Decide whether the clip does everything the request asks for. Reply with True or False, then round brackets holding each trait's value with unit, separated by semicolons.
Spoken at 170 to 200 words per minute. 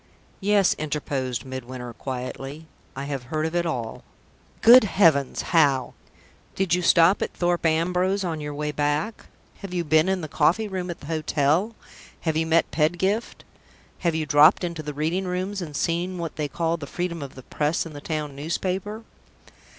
True (175 wpm)